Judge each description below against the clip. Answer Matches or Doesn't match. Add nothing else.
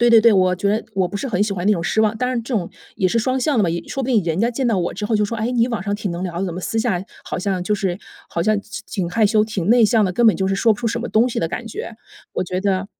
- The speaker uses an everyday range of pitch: Matches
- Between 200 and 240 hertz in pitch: Matches